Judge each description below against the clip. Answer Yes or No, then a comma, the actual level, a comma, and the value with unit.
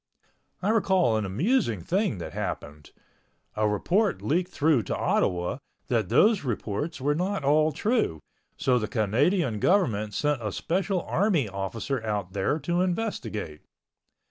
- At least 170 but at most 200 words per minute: No, average, 140 wpm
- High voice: No, medium, 140 Hz